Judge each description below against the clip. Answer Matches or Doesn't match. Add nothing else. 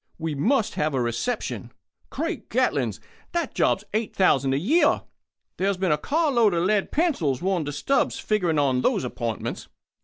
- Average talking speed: Matches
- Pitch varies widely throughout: Matches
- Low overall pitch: Doesn't match